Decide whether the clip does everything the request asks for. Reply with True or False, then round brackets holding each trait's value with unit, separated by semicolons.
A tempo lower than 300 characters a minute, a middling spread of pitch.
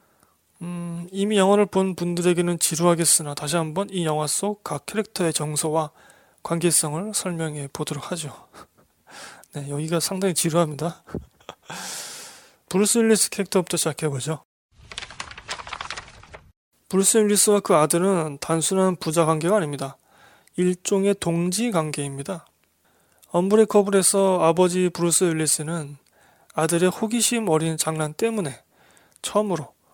True (285 characters per minute; 3.8 semitones)